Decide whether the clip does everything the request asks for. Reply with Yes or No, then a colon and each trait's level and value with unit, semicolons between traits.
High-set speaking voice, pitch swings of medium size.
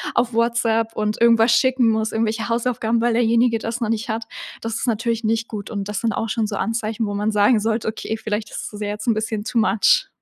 No: high, 225 Hz; narrow, 1.3 semitones